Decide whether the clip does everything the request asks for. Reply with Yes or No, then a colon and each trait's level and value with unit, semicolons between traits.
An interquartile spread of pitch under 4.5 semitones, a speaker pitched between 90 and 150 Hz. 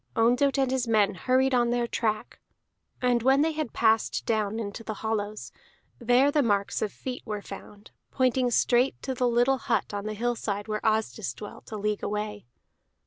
No: average, 3.1 semitones; high, 225 Hz